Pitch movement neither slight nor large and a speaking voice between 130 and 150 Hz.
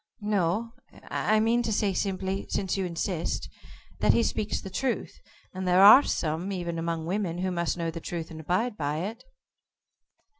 No: average, 3.7 semitones; medium, 185 Hz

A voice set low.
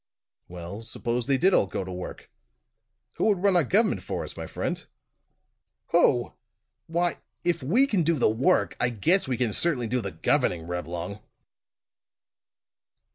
Yes: low, 125 Hz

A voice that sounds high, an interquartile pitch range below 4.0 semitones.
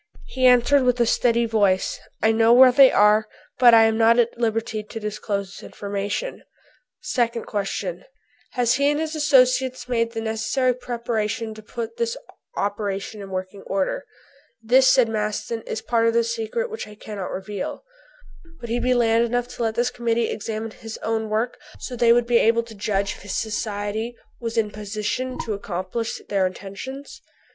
Yes: high, 225 Hz; narrow, 2.5 semitones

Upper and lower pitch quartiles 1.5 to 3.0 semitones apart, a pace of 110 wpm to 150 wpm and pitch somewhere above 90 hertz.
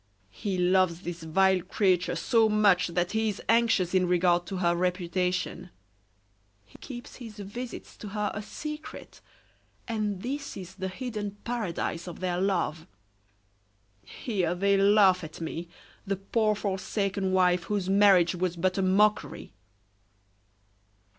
Yes: average, 2.7 semitones; slow, 135 wpm; high, 190 Hz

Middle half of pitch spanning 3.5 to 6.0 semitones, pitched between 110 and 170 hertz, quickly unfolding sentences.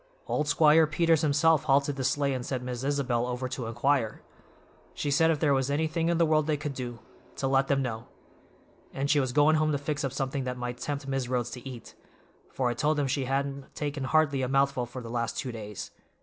No: average, 2.8 semitones; low, 135 Hz; fast, 225 wpm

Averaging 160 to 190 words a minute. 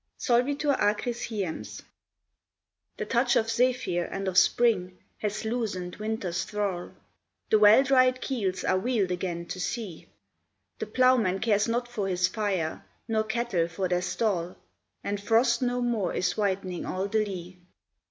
No: average, 150 wpm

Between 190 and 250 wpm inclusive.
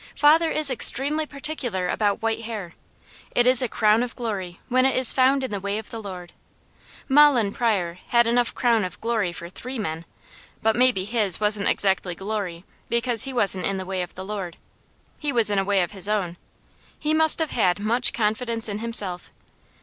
Yes: average, 195 wpm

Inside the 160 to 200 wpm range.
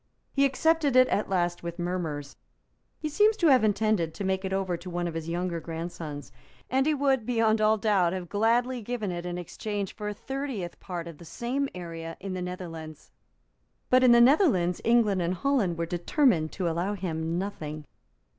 Yes: average, 190 wpm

